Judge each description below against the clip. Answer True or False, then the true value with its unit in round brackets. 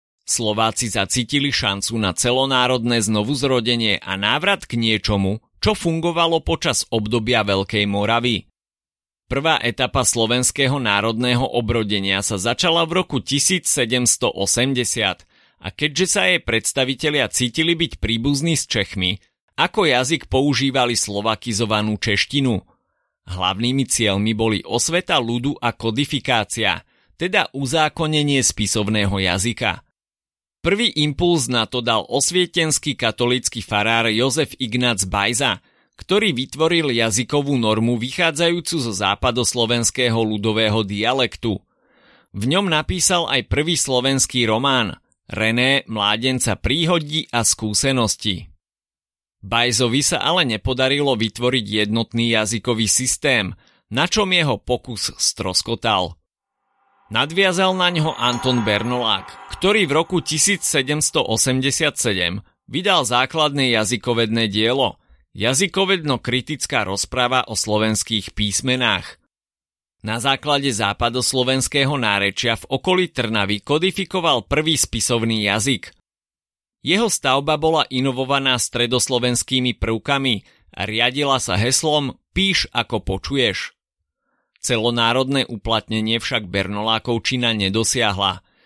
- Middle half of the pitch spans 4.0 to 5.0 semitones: True (4.5 semitones)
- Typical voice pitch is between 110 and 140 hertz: True (120 Hz)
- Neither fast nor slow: False (95 wpm)